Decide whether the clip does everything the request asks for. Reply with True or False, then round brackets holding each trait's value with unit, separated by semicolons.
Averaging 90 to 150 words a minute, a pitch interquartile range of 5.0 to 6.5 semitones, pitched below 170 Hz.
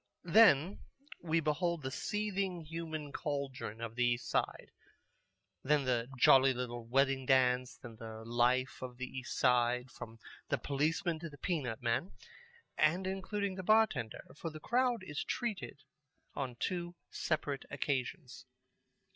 True (140 wpm; 5.5 semitones; 140 Hz)